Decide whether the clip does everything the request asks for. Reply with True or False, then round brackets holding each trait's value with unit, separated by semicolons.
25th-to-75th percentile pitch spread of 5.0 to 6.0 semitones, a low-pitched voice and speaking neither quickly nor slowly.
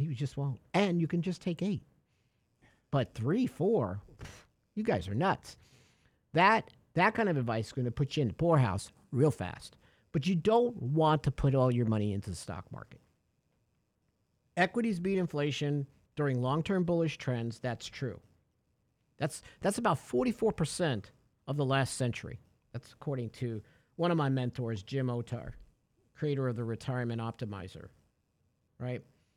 True (5.5 semitones; 130 Hz; 155 wpm)